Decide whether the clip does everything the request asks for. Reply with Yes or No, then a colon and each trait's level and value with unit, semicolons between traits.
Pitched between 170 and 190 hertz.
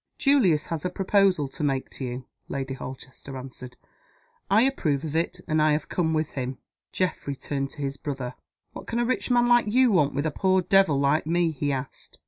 No: medium, 155 Hz